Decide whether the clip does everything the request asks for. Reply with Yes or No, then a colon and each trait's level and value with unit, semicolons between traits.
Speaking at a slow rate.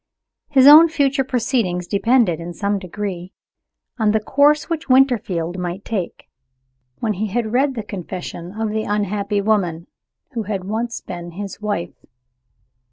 No: average, 145 wpm